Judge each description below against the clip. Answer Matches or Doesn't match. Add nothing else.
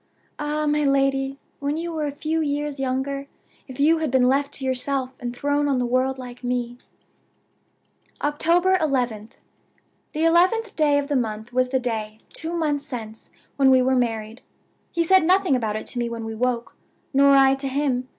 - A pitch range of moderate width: Matches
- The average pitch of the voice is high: Matches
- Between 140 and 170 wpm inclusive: Doesn't match